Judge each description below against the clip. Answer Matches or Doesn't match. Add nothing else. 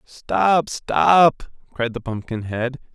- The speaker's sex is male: Matches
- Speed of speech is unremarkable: Doesn't match